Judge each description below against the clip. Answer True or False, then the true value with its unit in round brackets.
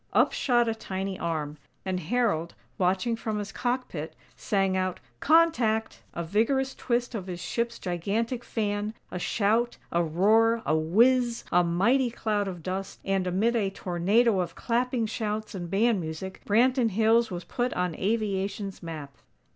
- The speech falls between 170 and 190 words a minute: False (155 wpm)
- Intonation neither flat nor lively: True (4.3 semitones)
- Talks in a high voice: True (205 Hz)